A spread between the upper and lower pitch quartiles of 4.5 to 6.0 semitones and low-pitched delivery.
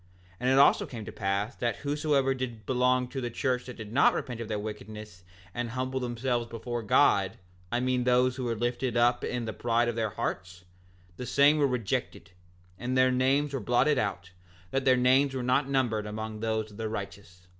No: average, 3.2 semitones; low, 120 Hz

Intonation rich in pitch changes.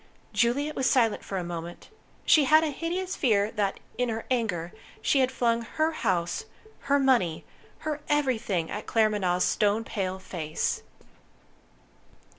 Yes: wide, 6.4 semitones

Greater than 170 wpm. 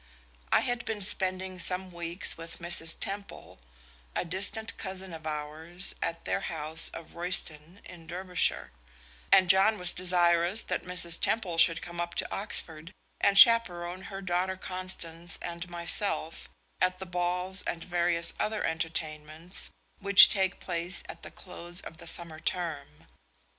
No: average, 145 wpm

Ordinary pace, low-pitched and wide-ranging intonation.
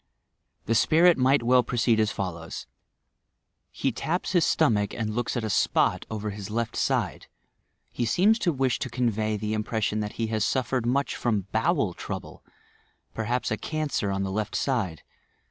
No: average, 165 wpm; low, 115 Hz; average, 3.4 semitones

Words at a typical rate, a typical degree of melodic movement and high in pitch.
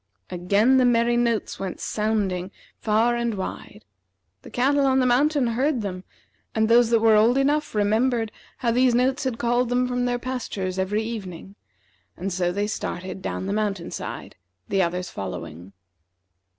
Yes: average, 165 wpm; average, 4.3 semitones; high, 225 Hz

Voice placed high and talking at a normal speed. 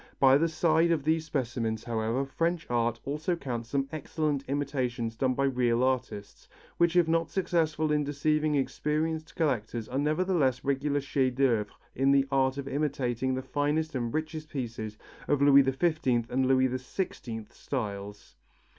No: low, 135 Hz; average, 155 wpm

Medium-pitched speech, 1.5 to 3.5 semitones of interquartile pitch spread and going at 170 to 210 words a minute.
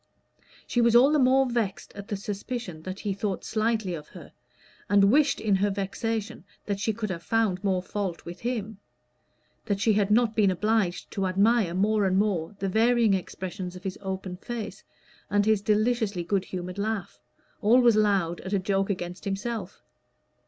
No: high, 205 Hz; average, 2.9 semitones; average, 175 wpm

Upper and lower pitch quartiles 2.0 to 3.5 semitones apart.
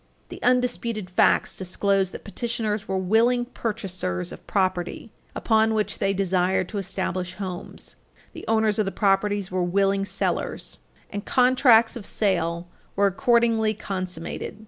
Yes: average, 3.1 semitones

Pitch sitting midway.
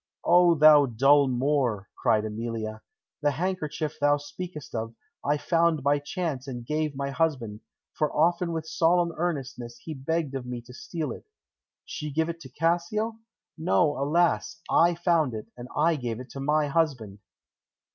Yes: medium, 150 Hz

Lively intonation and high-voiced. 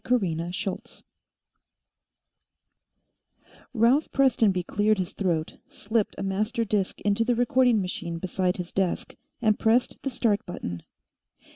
No: average, 3.8 semitones; high, 210 Hz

